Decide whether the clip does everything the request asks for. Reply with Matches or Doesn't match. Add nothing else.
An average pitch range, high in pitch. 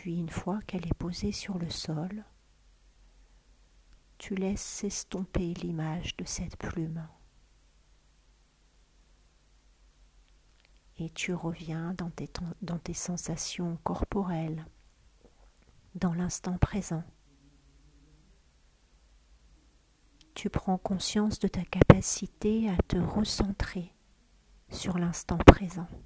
Doesn't match